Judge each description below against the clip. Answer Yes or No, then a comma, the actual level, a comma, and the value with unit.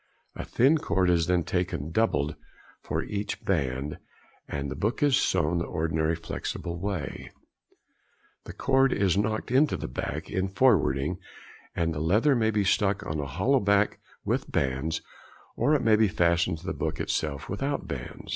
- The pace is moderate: Yes, average, 165 wpm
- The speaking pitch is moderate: No, very low, 90 Hz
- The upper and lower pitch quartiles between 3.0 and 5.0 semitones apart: No, wide, 5.5 semitones